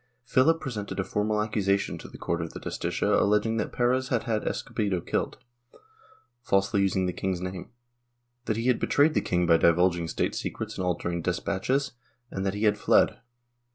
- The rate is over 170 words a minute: Yes, average, 180 wpm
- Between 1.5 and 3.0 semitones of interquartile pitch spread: No, average, 3.6 semitones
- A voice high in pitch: No, low, 100 Hz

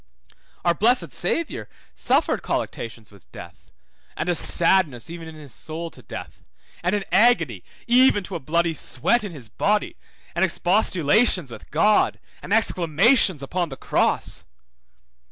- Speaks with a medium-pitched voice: Yes, medium, 170 Hz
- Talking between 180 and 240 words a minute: No, average, 140 wpm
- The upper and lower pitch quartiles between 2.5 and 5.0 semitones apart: No, wide, 5.6 semitones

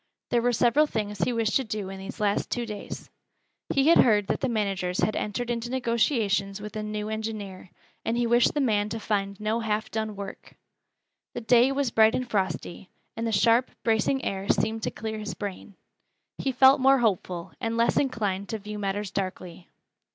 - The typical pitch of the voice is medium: No, high, 220 Hz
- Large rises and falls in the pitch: No, average, 2.8 semitones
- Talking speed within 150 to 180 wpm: No, average, 195 wpm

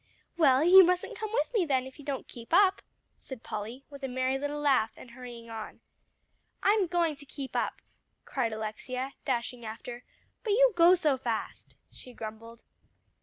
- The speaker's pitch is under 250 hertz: No, very high, 265 Hz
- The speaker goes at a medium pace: Yes, average, 170 wpm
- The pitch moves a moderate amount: No, wide, 6.1 semitones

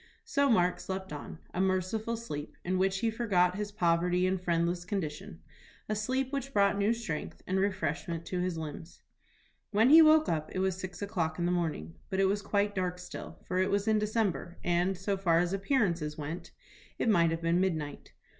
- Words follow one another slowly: No, average, 195 wpm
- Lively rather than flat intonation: No, average, 3.1 semitones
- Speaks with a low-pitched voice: No, medium, 185 Hz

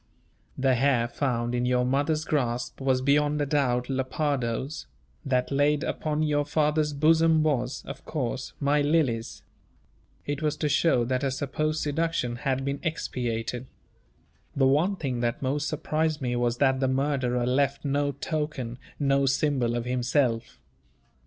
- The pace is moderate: Yes, average, 145 wpm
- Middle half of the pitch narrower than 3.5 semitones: Yes, average, 3.0 semitones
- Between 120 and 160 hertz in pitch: Yes, medium, 140 Hz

